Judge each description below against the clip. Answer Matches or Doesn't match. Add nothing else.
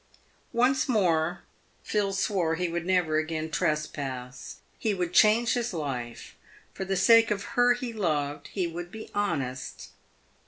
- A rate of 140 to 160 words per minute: Matches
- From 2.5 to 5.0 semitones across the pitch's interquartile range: Doesn't match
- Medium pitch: Matches